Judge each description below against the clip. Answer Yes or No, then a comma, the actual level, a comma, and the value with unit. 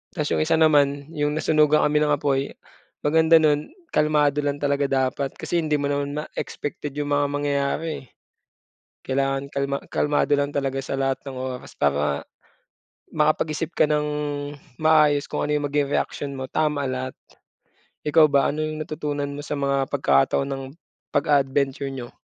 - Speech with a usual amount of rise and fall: No, narrow, 1.5 semitones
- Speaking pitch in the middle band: Yes, medium, 145 Hz